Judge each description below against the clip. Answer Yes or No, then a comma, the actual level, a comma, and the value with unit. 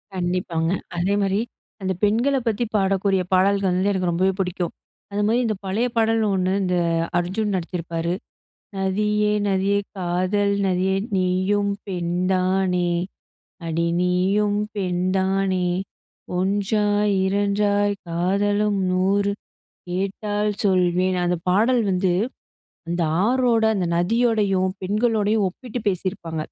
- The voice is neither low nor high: No, high, 195 Hz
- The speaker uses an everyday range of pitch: No, narrow, 2.1 semitones